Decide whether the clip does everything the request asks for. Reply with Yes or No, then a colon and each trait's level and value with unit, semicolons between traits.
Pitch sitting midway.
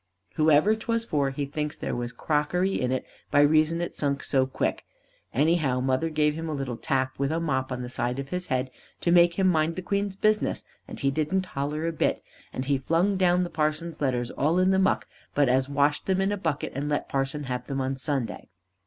Yes: medium, 150 Hz